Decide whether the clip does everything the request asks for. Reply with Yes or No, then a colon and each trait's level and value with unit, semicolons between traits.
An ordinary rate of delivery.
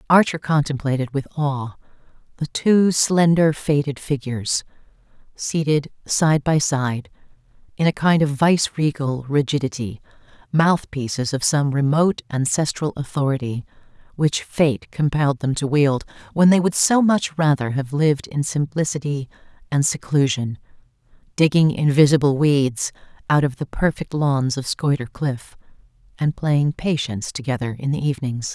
No: slow, 125 wpm